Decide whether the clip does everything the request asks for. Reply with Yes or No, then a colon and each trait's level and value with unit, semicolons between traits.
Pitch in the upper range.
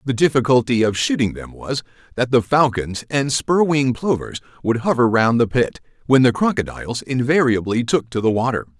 No: low, 125 Hz